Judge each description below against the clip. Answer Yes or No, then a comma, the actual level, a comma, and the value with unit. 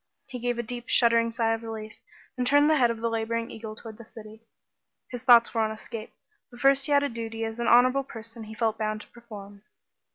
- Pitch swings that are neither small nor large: No, narrow, 1.7 semitones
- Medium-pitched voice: No, high, 230 Hz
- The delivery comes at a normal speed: No, fast, 235 wpm